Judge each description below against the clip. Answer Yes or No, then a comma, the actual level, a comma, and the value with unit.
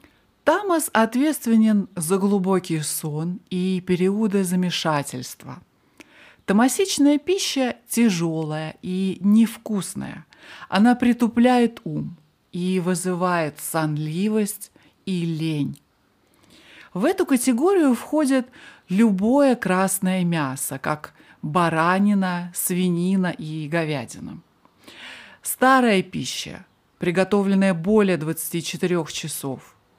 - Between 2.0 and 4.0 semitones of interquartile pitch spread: No, average, 5.2 semitones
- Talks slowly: Yes, slow, 80 wpm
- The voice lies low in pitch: No, medium, 185 Hz